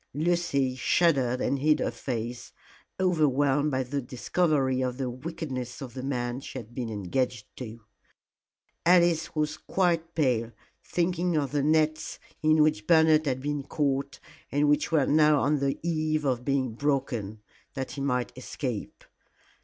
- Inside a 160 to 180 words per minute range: No, average, 150 wpm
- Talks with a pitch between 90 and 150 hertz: Yes, medium, 140 Hz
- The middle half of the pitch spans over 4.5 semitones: No, average, 3.5 semitones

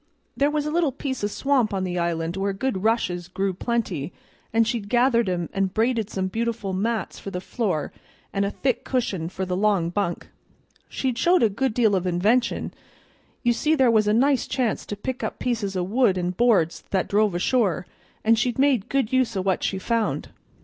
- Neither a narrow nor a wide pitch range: Yes, average, 4.5 semitones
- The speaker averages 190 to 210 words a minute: Yes, average, 200 wpm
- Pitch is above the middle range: Yes, high, 215 Hz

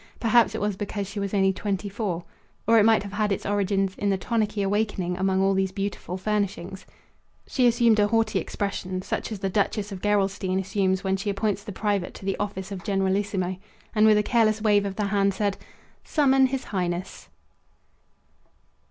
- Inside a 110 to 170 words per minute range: No, average, 185 wpm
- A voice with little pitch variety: Yes, narrow, 1.8 semitones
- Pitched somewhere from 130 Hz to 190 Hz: No, high, 200 Hz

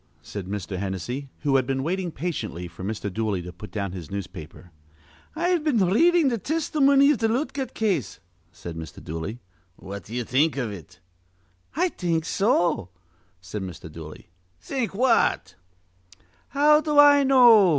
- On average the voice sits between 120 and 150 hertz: Yes, medium, 140 Hz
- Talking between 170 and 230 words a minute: No, average, 155 wpm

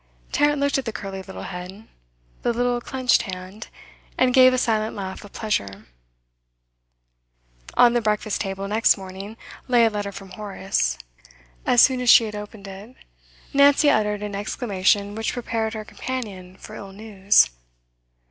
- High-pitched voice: Yes, high, 210 Hz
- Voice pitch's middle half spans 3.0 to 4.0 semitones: Yes, average, 3.6 semitones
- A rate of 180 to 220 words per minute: No, average, 155 wpm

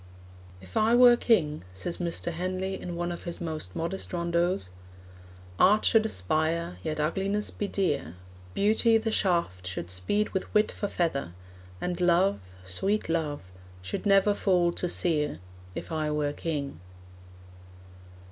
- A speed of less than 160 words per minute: Yes, average, 140 wpm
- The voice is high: No, medium, 170 Hz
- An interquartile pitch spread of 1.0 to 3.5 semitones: No, average, 4.6 semitones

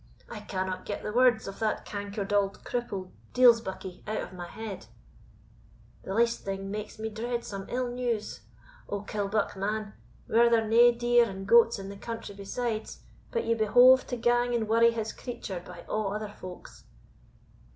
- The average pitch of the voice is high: Yes, high, 220 Hz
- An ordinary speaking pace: Yes, average, 170 wpm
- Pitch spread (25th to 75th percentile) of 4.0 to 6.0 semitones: No, average, 3.0 semitones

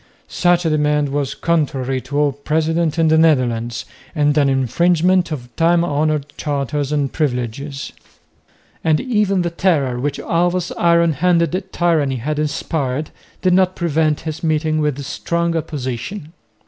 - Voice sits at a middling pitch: Yes, medium, 155 Hz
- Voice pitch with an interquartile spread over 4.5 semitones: No, average, 3.2 semitones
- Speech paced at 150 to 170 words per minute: No, average, 140 wpm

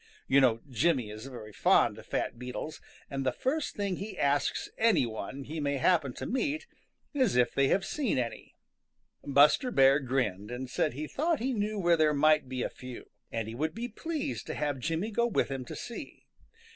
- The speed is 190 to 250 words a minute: Yes, average, 200 wpm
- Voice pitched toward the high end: No, medium, 145 Hz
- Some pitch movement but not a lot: No, wide, 8.5 semitones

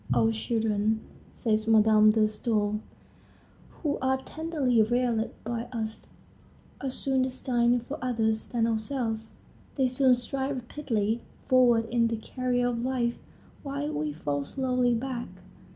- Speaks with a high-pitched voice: Yes, high, 235 Hz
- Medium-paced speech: No, slow, 130 wpm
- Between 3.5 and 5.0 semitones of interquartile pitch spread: No, average, 2.7 semitones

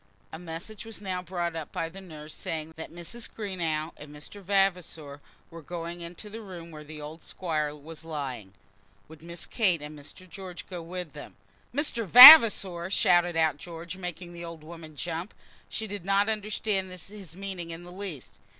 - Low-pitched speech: No, medium, 170 Hz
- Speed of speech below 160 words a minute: No, average, 175 wpm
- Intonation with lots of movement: No, average, 3.3 semitones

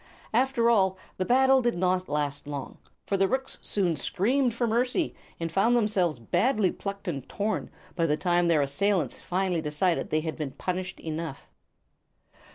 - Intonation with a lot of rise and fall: Yes, wide, 5.9 semitones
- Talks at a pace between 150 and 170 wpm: Yes, average, 165 wpm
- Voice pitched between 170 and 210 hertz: Yes, medium, 185 Hz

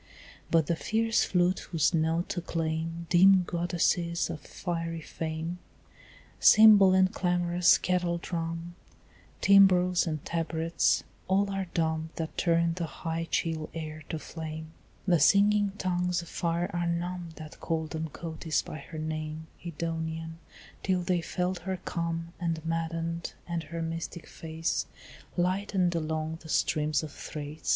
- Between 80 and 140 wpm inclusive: Yes, slow, 135 wpm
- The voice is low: No, medium, 170 Hz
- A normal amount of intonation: No, narrow, 1.7 semitones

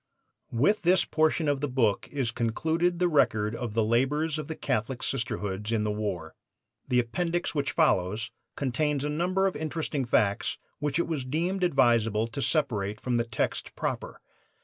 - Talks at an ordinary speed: Yes, average, 170 wpm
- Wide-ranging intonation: Yes, wide, 5.9 semitones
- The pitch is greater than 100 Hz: Yes, low, 135 Hz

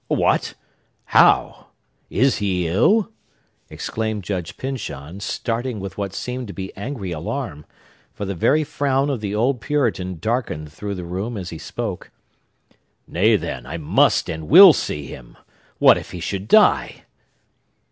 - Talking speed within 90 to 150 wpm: Yes, average, 145 wpm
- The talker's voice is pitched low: Yes, low, 100 Hz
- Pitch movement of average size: No, wide, 6.0 semitones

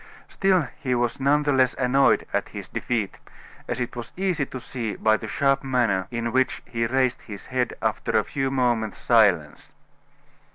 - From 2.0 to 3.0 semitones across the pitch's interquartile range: Yes, narrow, 2.6 semitones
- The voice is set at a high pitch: No, low, 125 Hz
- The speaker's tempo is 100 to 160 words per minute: No, average, 175 wpm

